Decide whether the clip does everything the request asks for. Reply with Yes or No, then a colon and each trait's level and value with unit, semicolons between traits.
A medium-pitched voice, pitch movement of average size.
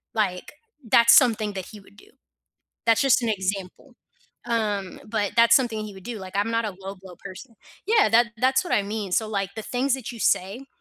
No: high, 215 Hz; average, 3.0 semitones